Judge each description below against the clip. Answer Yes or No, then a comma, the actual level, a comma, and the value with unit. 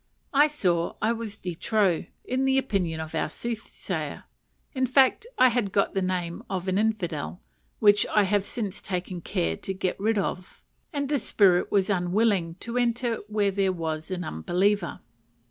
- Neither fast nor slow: Yes, average, 170 wpm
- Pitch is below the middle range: No, high, 200 Hz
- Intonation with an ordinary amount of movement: Yes, average, 4.2 semitones